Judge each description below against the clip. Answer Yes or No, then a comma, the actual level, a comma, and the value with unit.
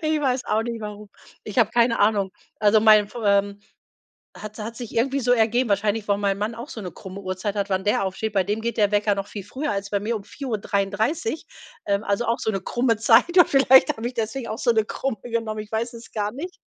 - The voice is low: No, high, 220 Hz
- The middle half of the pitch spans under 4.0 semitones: Yes, average, 2.7 semitones